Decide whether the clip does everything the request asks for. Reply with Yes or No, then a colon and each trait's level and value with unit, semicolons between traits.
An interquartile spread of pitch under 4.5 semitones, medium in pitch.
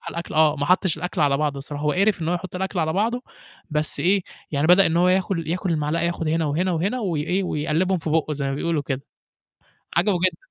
Yes: average, 3.4 semitones; medium, 165 Hz